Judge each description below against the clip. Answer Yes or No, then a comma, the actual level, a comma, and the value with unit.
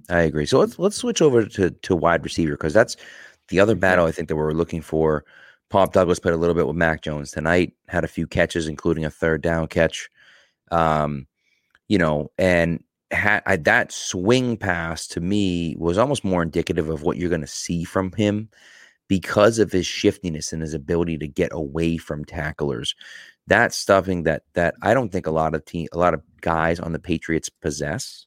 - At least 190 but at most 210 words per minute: Yes, average, 200 wpm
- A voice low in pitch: Yes, very low, 85 Hz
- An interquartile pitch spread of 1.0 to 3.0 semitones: Yes, narrow, 2.6 semitones